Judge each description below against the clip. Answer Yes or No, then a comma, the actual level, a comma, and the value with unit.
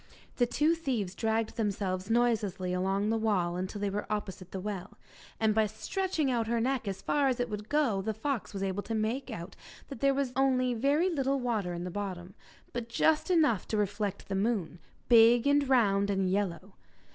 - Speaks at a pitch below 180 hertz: No, high, 220 Hz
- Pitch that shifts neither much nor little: Yes, average, 4.5 semitones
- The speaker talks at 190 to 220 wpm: Yes, average, 195 wpm